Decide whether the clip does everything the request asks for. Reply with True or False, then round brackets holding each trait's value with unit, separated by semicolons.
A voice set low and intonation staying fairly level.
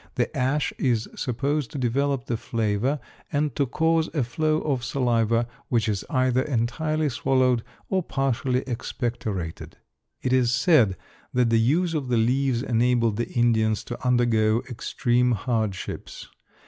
False (125 Hz; 3.1 semitones)